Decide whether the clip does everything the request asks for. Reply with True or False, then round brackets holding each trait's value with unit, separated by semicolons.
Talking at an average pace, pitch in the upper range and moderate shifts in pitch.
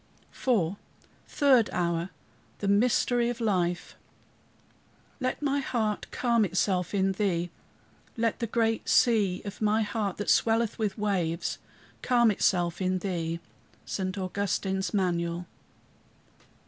False (115 wpm; 200 Hz; 3.9 semitones)